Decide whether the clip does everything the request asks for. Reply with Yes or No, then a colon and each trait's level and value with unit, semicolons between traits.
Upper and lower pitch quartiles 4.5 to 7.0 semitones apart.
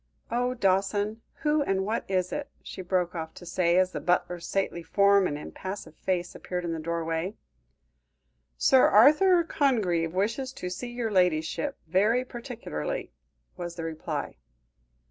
Yes: wide, 5.5 semitones